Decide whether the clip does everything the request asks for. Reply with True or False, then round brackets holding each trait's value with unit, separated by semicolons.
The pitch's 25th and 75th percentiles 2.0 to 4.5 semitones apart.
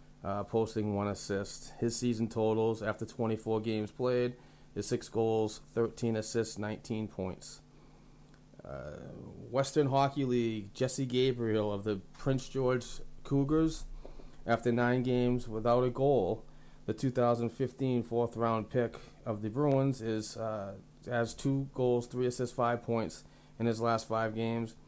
True (2.4 semitones)